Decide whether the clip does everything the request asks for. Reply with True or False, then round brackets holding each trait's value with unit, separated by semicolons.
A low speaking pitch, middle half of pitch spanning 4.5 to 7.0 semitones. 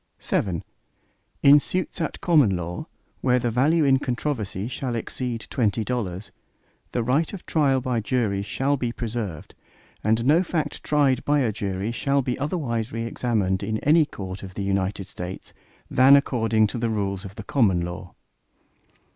True (115 Hz; 5.4 semitones)